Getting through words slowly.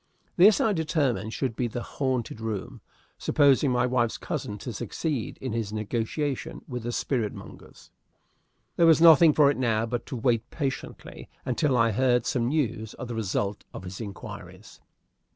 No: average, 165 wpm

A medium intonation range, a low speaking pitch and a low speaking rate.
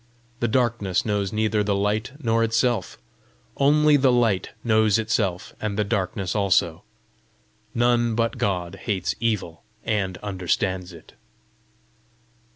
Yes: average, 3.4 semitones; low, 105 Hz; slow, 120 wpm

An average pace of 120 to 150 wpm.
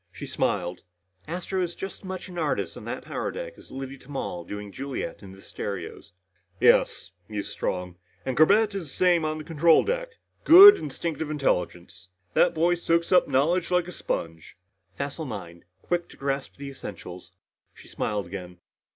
No: average, 170 wpm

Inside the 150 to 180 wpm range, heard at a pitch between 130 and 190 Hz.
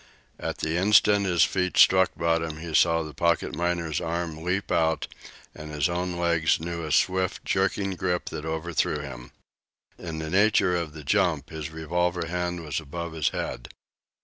No: average, 170 wpm; very low, 85 Hz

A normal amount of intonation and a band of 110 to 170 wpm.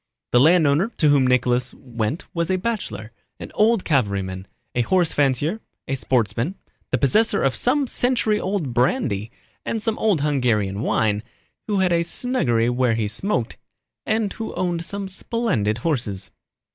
No: wide, 9.0 semitones; average, 150 wpm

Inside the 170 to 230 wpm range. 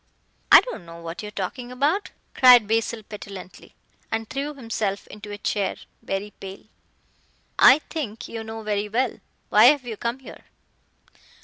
No: average, 155 wpm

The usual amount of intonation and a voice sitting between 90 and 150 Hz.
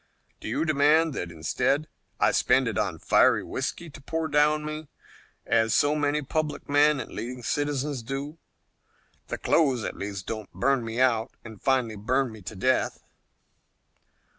Yes: average, 4.9 semitones; low, 135 Hz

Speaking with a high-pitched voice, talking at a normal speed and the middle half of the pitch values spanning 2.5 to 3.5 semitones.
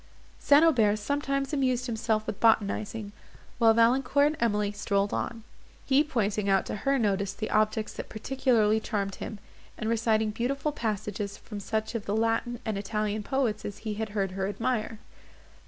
Yes: high, 220 Hz; average, 165 wpm; average, 2.9 semitones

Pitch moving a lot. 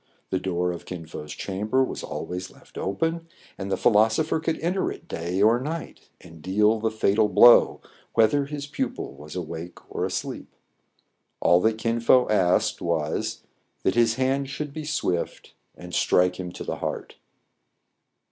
Yes: wide, 6.5 semitones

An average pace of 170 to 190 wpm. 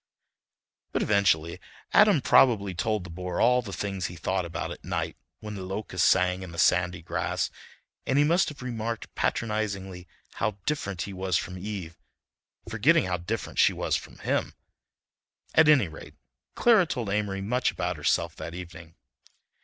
No: average, 160 wpm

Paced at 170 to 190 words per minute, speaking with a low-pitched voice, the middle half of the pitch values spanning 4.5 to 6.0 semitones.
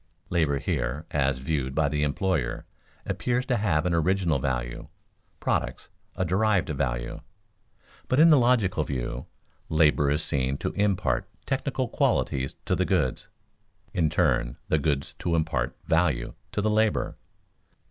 No: average, 140 wpm; very low, 80 Hz; wide, 5.6 semitones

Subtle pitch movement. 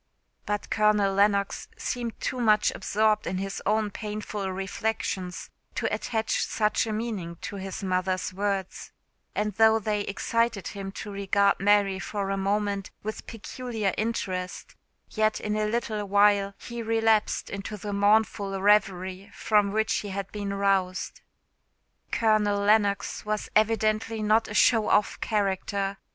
Yes: narrow, 1.6 semitones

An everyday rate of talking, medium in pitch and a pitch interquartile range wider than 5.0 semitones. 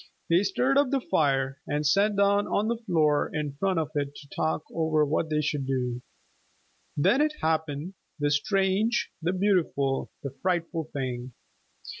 Yes: average, 160 wpm; medium, 160 Hz; wide, 5.4 semitones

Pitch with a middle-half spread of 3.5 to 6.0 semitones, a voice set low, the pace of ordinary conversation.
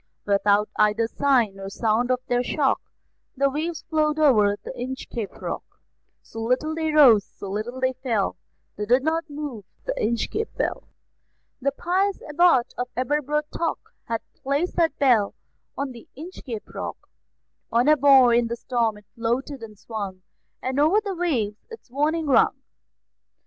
No: average, 5.1 semitones; very high, 260 Hz; average, 155 wpm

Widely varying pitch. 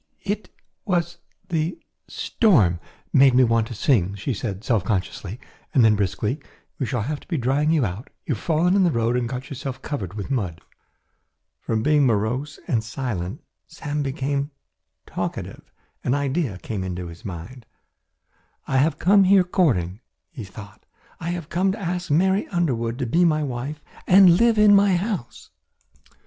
Yes: wide, 7.5 semitones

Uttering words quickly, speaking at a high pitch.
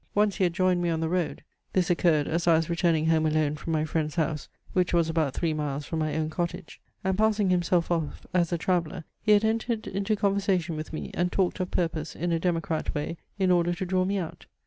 No: fast, 235 wpm; medium, 170 Hz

